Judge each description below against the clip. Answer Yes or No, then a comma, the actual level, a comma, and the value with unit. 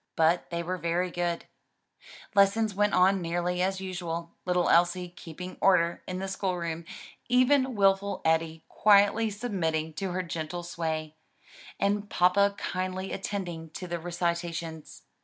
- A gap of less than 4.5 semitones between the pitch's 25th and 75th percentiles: Yes, narrow, 2.5 semitones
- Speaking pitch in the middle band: Yes, medium, 180 Hz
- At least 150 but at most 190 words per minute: No, average, 140 wpm